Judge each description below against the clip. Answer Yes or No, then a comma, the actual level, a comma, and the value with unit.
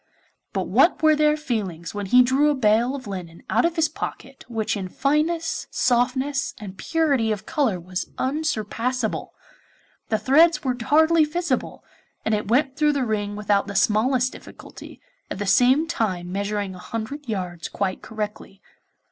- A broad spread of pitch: Yes, wide, 6.1 semitones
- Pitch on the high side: Yes, high, 240 Hz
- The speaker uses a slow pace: No, average, 160 wpm